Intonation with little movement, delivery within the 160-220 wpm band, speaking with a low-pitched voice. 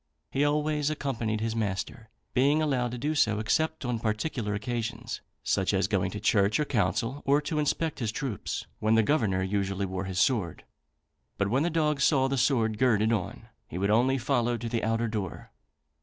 No: average, 4.8 semitones; average, 185 wpm; low, 115 Hz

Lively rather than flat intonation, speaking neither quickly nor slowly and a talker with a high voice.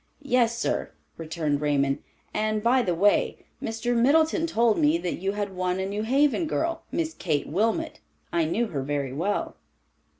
Yes: wide, 6.9 semitones; average, 160 wpm; high, 205 Hz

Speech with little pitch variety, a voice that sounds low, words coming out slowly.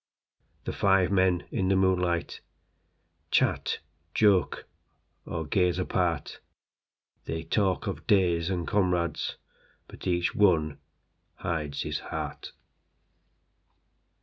Yes: narrow, 2.1 semitones; very low, 90 Hz; slow, 85 wpm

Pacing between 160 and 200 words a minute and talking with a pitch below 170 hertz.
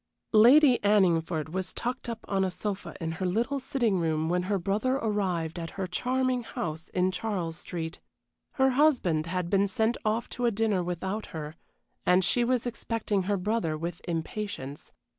No: average, 170 wpm; high, 195 Hz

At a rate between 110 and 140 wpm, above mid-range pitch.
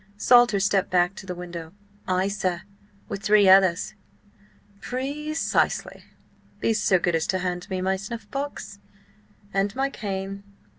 Yes: slow, 135 wpm; high, 195 Hz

